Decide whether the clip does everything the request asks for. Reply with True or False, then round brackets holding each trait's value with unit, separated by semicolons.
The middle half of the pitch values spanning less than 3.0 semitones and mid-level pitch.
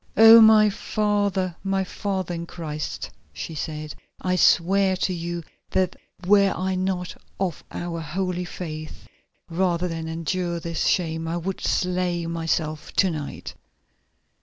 True (2.5 semitones; 180 Hz)